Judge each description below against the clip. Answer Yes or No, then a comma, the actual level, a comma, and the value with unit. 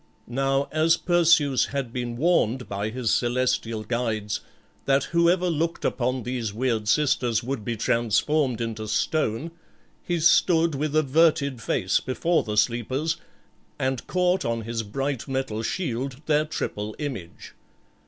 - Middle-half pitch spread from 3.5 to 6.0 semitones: Yes, average, 5.1 semitones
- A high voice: No, low, 130 Hz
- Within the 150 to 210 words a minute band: No, slow, 135 wpm